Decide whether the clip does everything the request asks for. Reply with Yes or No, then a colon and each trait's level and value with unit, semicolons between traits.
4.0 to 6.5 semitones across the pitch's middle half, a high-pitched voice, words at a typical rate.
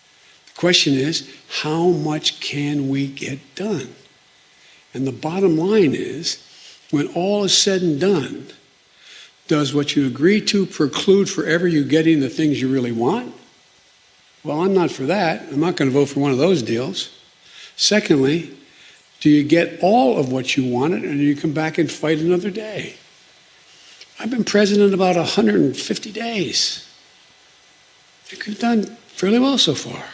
No: average, 5.2 semitones; medium, 165 Hz; average, 155 wpm